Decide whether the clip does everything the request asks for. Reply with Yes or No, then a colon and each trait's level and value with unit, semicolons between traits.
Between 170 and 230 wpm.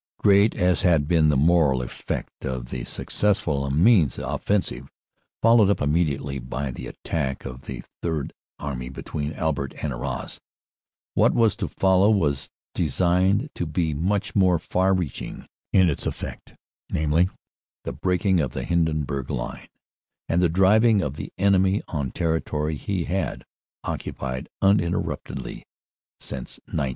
No: average, 140 wpm